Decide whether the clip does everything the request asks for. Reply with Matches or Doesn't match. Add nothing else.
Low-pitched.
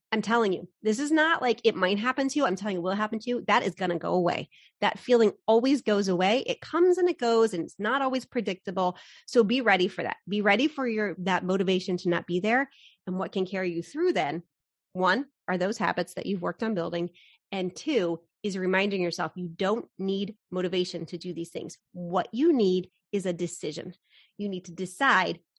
Doesn't match